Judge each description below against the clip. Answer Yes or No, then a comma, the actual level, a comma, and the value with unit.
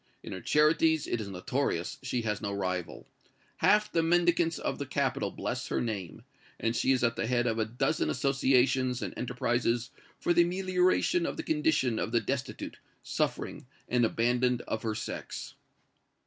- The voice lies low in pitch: Yes, low, 125 Hz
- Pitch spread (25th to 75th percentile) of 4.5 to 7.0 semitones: Yes, average, 5.1 semitones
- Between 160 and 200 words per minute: Yes, average, 170 wpm